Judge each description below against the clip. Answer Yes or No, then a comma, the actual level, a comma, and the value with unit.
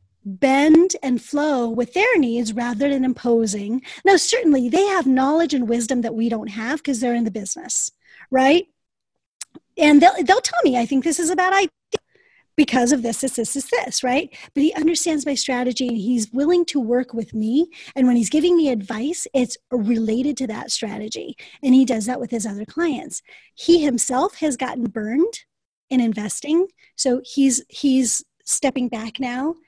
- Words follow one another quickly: No, average, 180 wpm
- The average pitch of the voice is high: Yes, very high, 265 Hz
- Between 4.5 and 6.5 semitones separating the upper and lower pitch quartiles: Yes, average, 5.0 semitones